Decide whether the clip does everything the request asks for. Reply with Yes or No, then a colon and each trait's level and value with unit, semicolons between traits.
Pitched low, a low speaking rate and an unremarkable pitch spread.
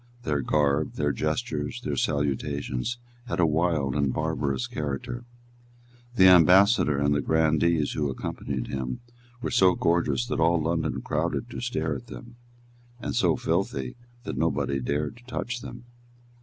No: very low, 75 Hz; average, 145 wpm; average, 4.0 semitones